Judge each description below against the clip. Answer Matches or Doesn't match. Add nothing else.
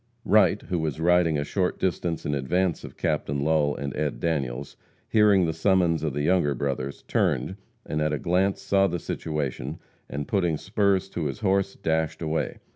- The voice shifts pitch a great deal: Doesn't match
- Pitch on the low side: Matches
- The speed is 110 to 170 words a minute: Doesn't match